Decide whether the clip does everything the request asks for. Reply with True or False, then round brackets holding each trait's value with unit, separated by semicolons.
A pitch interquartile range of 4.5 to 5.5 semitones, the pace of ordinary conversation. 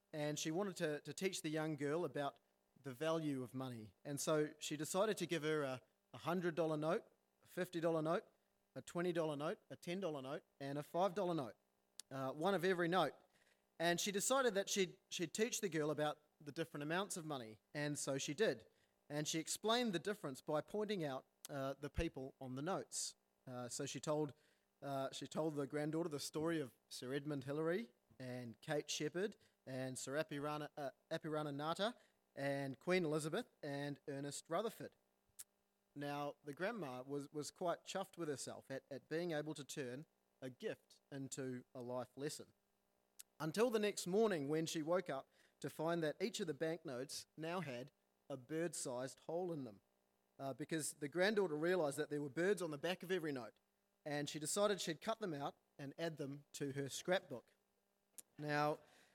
False (3.7 semitones; 180 wpm)